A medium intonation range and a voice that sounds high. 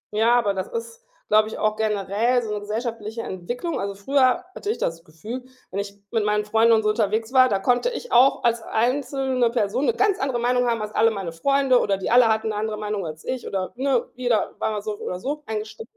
Yes: average, 3.2 semitones; high, 225 Hz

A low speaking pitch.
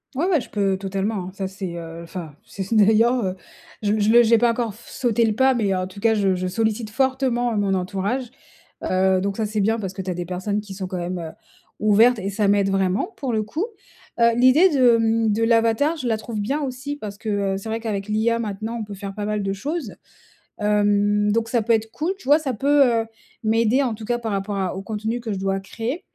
No: high, 215 Hz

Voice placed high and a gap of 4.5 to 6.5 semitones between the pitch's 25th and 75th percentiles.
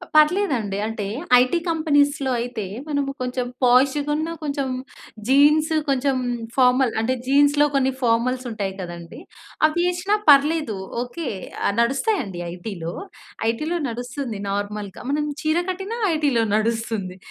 Yes: very high, 265 Hz; average, 5.0 semitones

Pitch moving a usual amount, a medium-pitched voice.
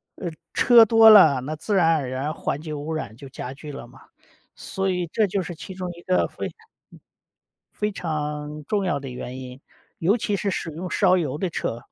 Yes: average, 5.0 semitones; medium, 160 Hz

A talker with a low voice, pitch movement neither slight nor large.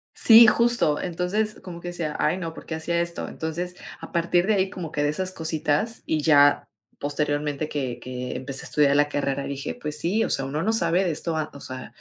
No: medium, 160 Hz; average, 3.5 semitones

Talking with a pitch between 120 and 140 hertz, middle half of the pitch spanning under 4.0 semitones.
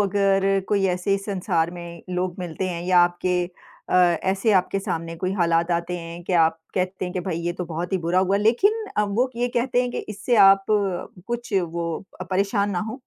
No: medium, 185 Hz; narrow, 2.6 semitones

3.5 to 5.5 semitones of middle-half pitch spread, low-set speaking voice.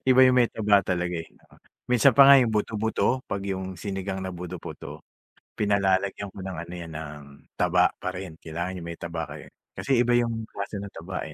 Yes: average, 4.1 semitones; very low, 95 Hz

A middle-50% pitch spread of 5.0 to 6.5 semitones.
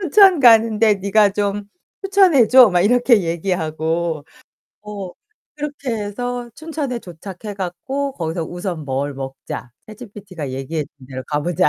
No: wide, 6.9 semitones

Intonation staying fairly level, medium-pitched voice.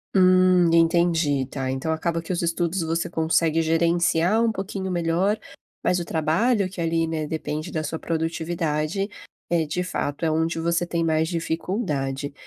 Yes: narrow, 1.7 semitones; medium, 165 Hz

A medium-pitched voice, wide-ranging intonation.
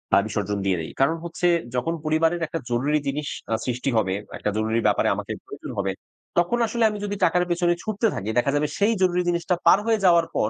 Yes: medium, 160 Hz; wide, 6.9 semitones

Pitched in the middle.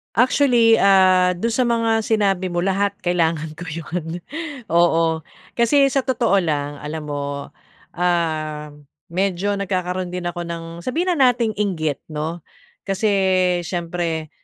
Yes: medium, 180 Hz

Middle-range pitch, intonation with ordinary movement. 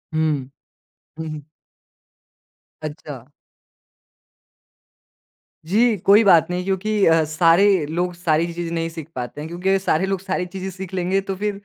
Yes: medium, 175 Hz; average, 3.4 semitones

